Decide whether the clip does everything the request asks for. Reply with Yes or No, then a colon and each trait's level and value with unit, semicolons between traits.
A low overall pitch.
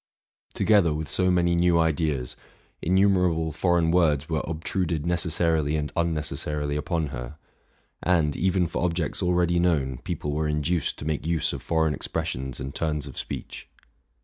Yes: very low, 80 Hz